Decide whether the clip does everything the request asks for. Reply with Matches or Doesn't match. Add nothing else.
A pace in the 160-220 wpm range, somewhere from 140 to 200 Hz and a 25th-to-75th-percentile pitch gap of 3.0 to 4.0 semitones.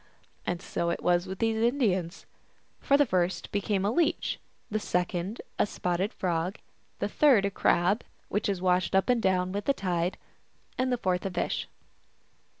Matches